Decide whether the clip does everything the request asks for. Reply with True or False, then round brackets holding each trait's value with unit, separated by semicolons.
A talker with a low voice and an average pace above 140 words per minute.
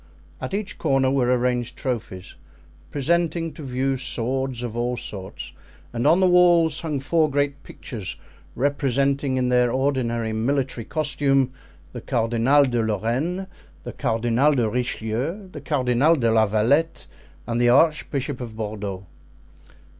False (130 Hz; 135 wpm)